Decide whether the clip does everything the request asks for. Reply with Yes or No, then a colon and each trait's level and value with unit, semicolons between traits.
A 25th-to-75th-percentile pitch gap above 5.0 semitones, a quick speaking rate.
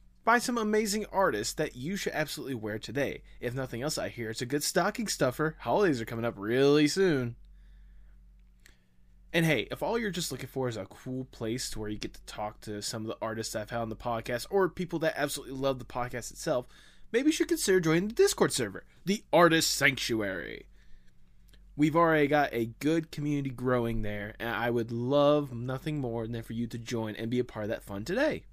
Yes: wide, 5.6 semitones; fast, 210 wpm